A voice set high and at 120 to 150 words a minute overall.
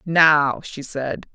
No: medium, 150 Hz; slow, 135 wpm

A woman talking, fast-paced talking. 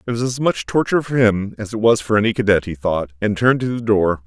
No: male; fast, 280 wpm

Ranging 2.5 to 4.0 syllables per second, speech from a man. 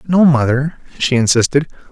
No: 5.3 syllables/s; male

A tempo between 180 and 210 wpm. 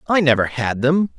Yes: fast, 205 wpm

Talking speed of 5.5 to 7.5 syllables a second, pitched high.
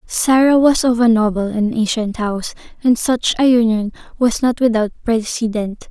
No: 4.7 syllables/s; high, 230 Hz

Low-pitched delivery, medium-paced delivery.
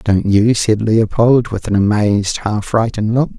Yes: low, 110 Hz; average, 175 wpm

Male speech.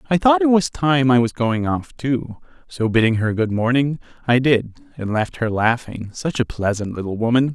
Yes: male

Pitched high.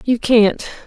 Yes: high, 230 Hz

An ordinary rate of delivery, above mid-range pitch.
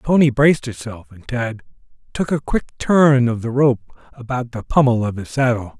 No: average, 195 wpm; low, 125 Hz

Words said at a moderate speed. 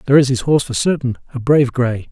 No: fast, 225 wpm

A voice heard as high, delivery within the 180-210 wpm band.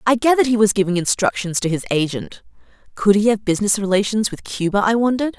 Yes: high, 210 Hz; average, 200 wpm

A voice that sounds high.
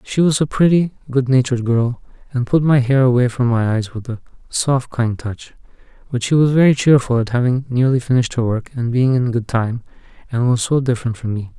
No: low, 125 Hz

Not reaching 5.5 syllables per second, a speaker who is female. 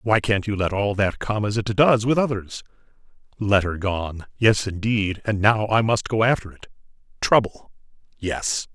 No: 4.5 syllables/s; male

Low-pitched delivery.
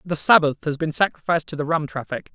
No: medium, 155 Hz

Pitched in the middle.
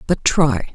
Yes: medium, 165 Hz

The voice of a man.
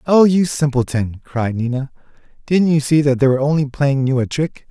Yes: male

